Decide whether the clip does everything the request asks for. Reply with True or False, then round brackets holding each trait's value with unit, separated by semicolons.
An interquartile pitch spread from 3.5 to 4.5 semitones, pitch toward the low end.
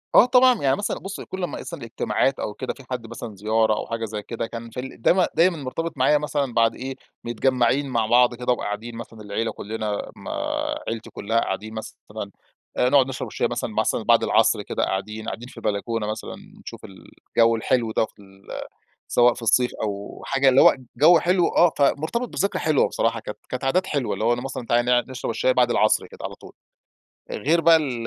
True (3.8 semitones; 120 Hz)